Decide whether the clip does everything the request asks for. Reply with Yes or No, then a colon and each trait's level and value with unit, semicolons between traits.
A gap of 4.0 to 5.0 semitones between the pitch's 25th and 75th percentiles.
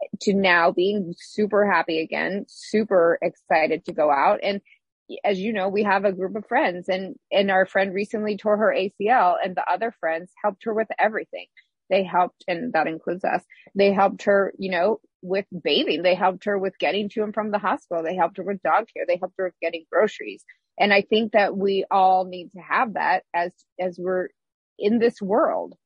No: narrow, 2.5 semitones